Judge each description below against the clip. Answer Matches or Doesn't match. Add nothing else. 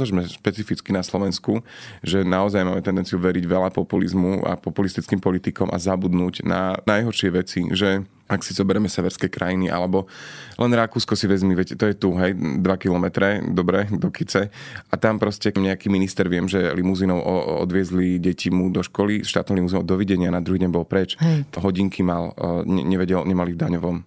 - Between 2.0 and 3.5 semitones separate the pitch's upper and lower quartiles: Doesn't match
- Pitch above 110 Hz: Doesn't match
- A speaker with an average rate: Doesn't match